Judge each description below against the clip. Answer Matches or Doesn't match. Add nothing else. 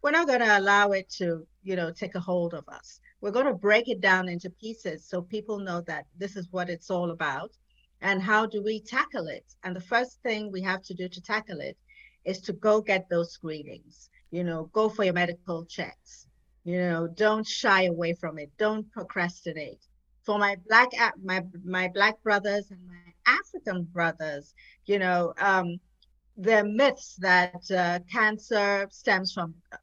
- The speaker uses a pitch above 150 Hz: Matches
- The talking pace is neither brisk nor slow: Matches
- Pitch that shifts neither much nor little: Matches